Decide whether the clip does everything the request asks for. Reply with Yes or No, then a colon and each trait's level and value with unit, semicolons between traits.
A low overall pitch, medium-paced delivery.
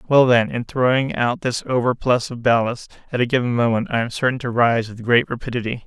No: low, 120 Hz; fast, 215 wpm